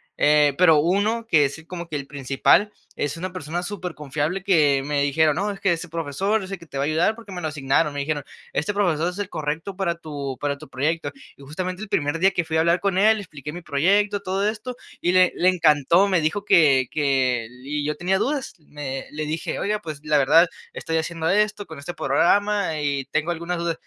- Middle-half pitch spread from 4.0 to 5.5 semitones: Yes, average, 4.3 semitones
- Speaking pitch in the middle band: Yes, medium, 165 Hz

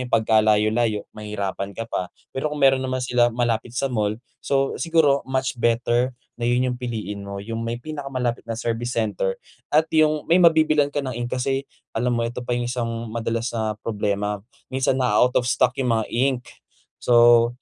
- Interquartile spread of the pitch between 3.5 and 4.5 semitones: No, narrow, 2.6 semitones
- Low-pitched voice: Yes, low, 120 Hz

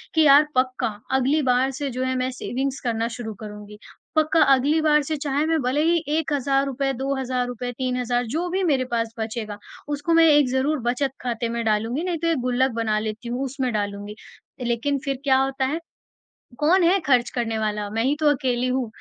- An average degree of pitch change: Yes, average, 3.5 semitones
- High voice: Yes, very high, 260 Hz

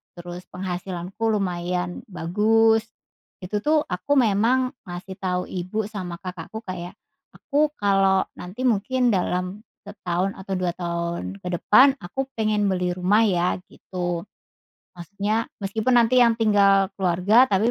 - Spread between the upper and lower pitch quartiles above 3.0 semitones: Yes, average, 3.6 semitones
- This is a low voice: No, high, 195 Hz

